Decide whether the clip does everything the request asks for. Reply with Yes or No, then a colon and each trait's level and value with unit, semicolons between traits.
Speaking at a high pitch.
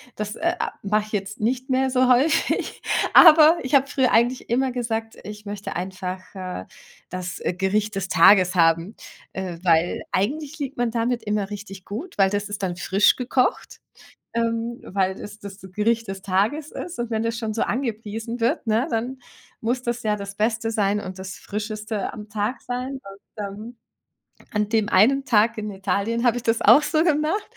Yes: high, 220 Hz